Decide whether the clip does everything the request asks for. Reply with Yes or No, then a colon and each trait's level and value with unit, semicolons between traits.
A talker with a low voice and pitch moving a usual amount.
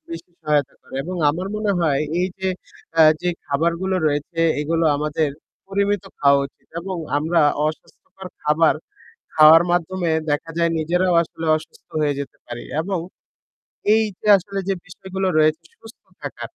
No: medium, 165 Hz; average, 3.6 semitones